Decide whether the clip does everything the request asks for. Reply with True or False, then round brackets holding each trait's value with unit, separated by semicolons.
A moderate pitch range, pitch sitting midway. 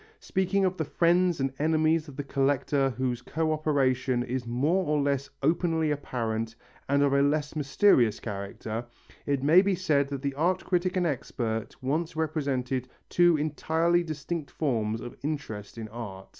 True (4.1 semitones; 145 Hz)